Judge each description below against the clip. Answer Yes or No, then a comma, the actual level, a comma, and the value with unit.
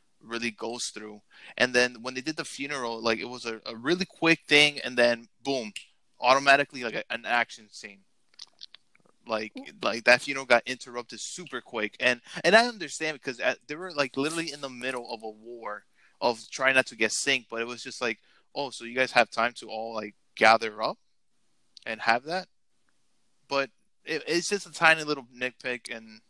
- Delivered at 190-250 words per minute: Yes, average, 195 wpm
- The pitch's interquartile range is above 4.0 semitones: No, average, 3.7 semitones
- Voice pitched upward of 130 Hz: No, low, 125 Hz